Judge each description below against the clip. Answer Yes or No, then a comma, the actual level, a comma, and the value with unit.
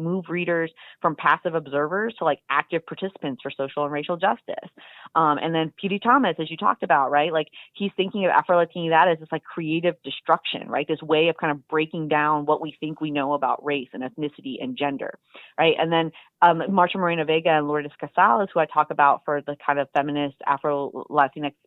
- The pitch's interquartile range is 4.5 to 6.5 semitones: No, average, 2.7 semitones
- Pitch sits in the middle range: Yes, medium, 155 Hz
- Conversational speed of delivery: No, fast, 210 wpm